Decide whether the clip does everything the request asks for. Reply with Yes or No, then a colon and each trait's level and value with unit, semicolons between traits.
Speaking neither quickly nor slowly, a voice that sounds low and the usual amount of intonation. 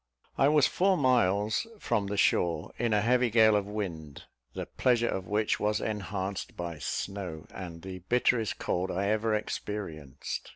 Yes: average, 160 wpm; low, 105 Hz; average, 3.7 semitones